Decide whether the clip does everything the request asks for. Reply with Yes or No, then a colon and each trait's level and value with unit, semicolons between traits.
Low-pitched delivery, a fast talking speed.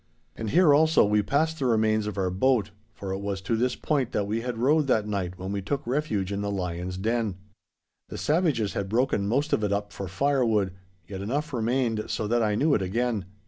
Yes: low, 110 Hz; fast, 220 wpm